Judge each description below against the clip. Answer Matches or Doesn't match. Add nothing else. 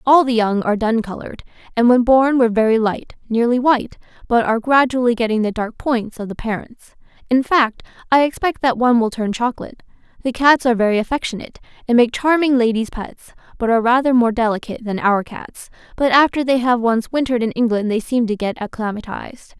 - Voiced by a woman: Matches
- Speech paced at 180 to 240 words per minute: Matches